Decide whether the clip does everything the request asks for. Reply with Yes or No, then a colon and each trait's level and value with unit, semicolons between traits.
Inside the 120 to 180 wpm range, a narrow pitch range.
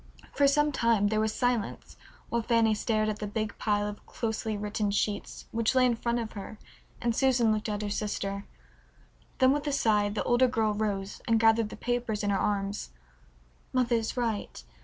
No: average, 190 wpm; narrow, 2.3 semitones